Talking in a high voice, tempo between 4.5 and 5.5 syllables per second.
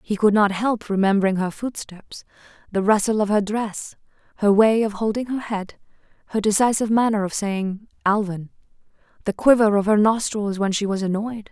Yes: high, 210 Hz; 5.2 syllables/s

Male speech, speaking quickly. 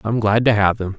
Yes: male; fast, 305 wpm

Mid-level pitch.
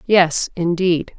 Yes: medium, 175 Hz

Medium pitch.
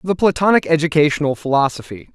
Yes: medium, 155 Hz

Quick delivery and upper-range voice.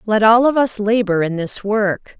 Yes: fast, 220 wpm; high, 210 Hz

